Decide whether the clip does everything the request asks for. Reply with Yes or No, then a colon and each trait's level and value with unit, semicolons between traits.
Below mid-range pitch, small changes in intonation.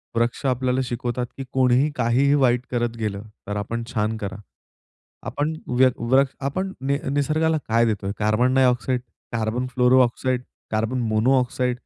Yes: low, 125 Hz; narrow, 2.2 semitones